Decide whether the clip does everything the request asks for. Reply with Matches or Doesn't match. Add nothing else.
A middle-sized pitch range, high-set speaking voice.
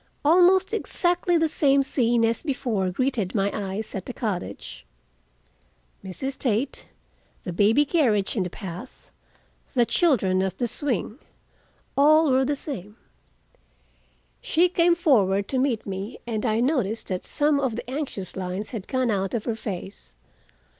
Doesn't match